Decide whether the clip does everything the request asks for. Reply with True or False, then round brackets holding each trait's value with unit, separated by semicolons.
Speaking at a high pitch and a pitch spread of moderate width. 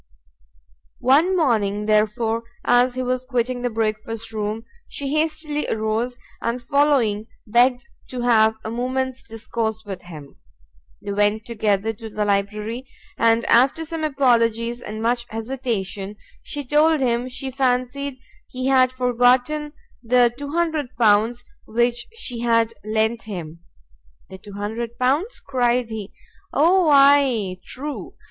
True (240 Hz; 3.1 semitones)